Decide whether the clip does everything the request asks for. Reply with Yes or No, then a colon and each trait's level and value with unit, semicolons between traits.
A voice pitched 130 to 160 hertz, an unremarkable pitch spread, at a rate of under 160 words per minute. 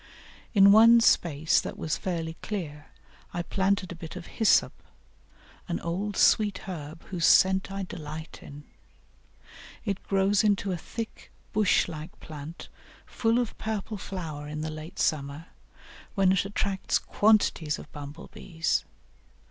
No: medium, 180 Hz; average, 4.1 semitones; average, 140 wpm